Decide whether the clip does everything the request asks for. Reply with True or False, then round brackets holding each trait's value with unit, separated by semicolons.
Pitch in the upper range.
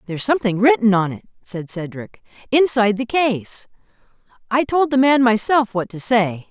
True (225 Hz)